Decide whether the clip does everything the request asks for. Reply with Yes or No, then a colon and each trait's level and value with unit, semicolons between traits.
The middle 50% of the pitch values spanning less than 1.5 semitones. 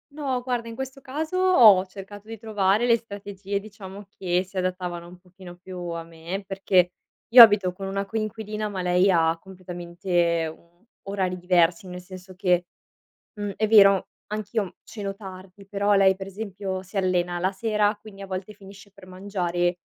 No: narrow, 2.4 semitones